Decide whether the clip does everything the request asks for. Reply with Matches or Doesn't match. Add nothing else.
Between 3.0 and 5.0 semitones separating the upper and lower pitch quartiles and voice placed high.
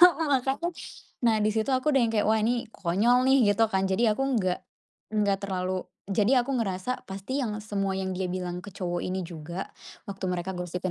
Matches